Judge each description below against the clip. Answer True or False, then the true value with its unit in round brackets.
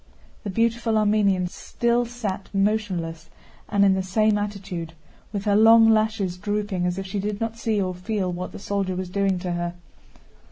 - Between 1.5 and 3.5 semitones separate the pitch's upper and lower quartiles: True (2.9 semitones)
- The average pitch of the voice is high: True (200 Hz)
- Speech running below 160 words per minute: False (175 wpm)